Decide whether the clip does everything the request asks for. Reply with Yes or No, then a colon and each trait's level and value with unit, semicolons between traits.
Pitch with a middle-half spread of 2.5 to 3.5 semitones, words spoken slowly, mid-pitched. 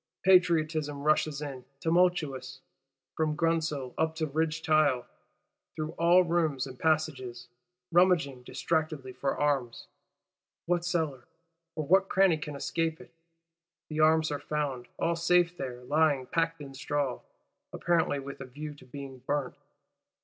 Yes: average, 3.2 semitones; slow, 130 wpm; medium, 155 Hz